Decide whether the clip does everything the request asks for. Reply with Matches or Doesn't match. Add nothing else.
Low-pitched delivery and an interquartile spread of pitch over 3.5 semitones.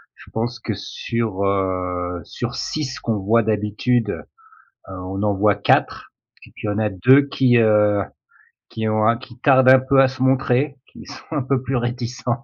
Matches